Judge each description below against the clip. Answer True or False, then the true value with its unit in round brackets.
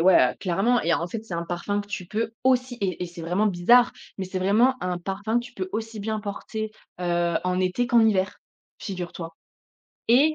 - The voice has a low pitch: False (200 Hz)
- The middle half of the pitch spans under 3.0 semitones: False (4.1 semitones)